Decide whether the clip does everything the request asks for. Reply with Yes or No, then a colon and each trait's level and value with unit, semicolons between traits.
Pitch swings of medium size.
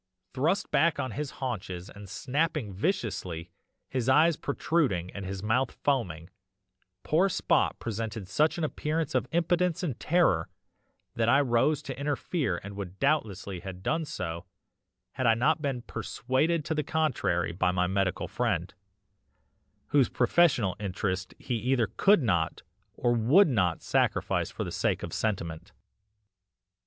No: wide, 7.8 semitones